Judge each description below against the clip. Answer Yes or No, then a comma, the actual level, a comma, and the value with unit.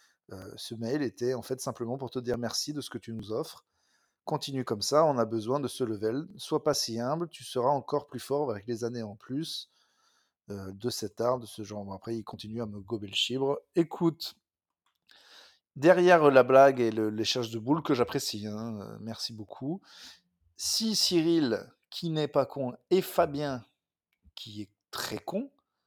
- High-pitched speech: No, low, 125 Hz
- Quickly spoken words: No, average, 195 wpm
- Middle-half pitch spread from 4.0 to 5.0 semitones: Yes, average, 4.6 semitones